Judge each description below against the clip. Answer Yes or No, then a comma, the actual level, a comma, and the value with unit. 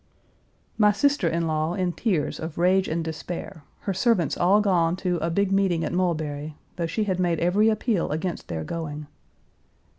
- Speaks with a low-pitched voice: No, medium, 175 Hz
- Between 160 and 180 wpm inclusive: Yes, average, 175 wpm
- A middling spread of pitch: Yes, average, 3.2 semitones